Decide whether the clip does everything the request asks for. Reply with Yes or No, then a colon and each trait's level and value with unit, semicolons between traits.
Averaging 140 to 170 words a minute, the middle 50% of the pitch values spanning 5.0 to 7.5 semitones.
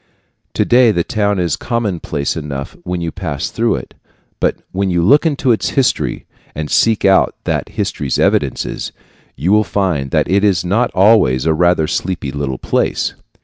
Yes: average, 165 wpm; wide, 5.4 semitones